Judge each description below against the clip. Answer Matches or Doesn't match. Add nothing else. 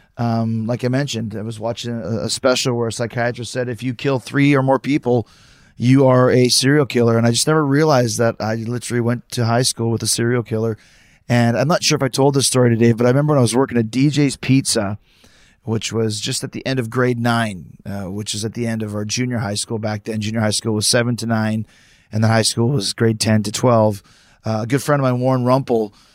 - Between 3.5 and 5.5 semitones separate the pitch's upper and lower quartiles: Doesn't match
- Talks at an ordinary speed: Doesn't match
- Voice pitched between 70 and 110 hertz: Doesn't match